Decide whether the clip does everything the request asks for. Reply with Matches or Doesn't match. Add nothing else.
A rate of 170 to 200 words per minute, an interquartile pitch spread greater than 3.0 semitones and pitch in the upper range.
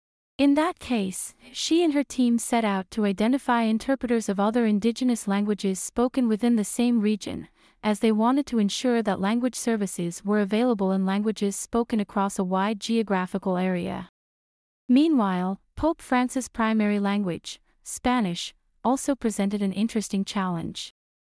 Doesn't match